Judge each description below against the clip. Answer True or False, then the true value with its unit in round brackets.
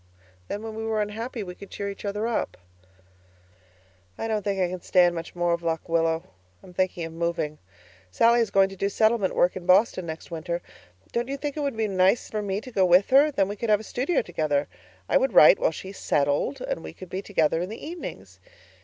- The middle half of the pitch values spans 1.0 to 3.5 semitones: False (4.3 semitones)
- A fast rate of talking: True (225 wpm)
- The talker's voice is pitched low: False (195 Hz)